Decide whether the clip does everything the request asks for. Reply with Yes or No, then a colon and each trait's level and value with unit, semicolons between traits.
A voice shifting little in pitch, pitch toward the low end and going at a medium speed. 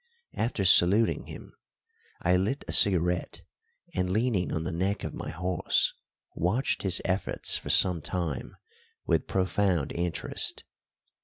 No: narrow, 2.2 semitones; very low, 90 Hz; slow, 130 wpm